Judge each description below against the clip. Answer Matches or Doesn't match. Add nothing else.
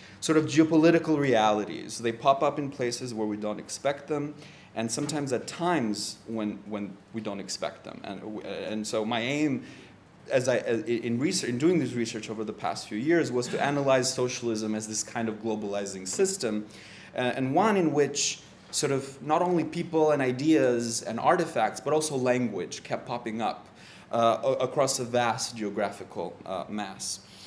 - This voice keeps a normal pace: Matches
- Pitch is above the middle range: Doesn't match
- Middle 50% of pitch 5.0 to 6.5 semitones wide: Matches